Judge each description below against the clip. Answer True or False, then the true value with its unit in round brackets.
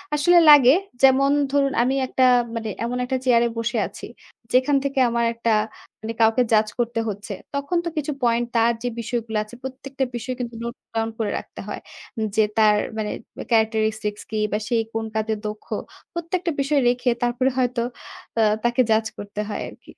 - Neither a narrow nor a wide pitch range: True (3.1 semitones)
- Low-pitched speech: False (235 Hz)